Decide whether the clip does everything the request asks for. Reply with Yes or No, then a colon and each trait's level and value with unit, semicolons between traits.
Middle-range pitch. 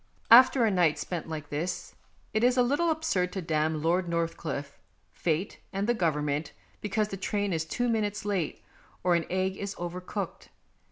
Yes: medium, 180 Hz